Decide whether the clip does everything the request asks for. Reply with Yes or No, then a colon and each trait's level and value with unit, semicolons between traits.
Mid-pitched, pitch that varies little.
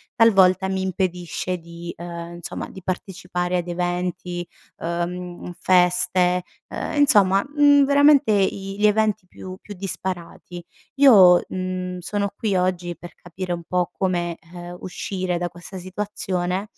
Yes: medium, 180 Hz; narrow, 1.7 semitones